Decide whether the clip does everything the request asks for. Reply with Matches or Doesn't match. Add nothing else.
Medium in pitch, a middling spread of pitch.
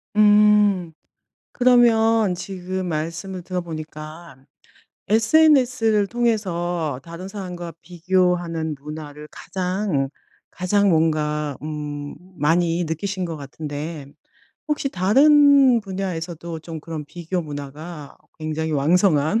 Matches